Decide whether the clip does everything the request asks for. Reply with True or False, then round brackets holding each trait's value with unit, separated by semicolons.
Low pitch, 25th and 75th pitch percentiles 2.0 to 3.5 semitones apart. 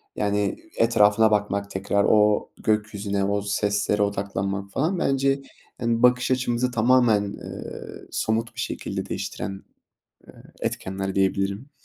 True (105 Hz; 2.8 semitones)